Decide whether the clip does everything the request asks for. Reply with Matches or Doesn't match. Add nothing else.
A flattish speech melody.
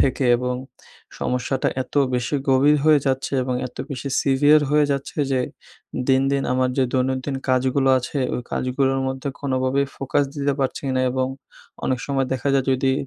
Matches